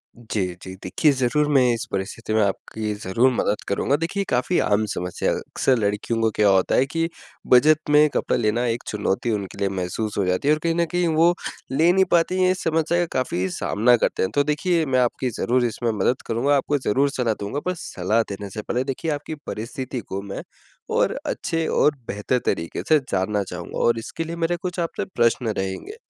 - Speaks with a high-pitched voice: No, low, 125 Hz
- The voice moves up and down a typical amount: No, wide, 6.6 semitones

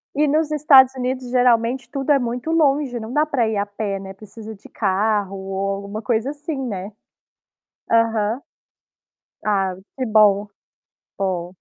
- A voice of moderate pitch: No, high, 230 Hz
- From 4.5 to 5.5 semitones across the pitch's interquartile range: Yes, average, 4.9 semitones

